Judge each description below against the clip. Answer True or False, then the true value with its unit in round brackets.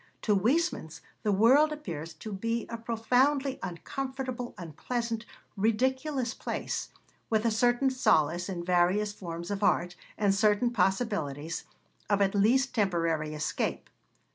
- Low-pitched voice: False (215 Hz)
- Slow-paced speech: True (125 wpm)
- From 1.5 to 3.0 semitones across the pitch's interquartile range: False (5.6 semitones)